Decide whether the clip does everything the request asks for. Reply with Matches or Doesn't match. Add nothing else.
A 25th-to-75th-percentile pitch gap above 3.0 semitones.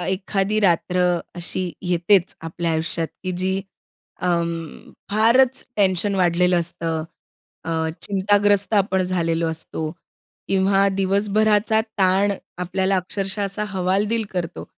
Doesn't match